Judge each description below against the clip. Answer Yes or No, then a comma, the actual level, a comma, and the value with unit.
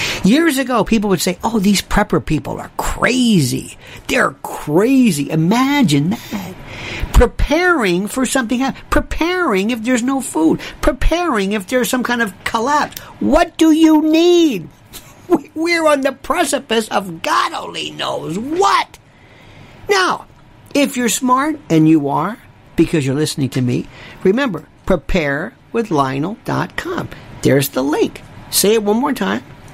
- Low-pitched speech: No, high, 240 Hz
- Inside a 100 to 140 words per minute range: Yes, slow, 135 wpm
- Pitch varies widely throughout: Yes, wide, 8.2 semitones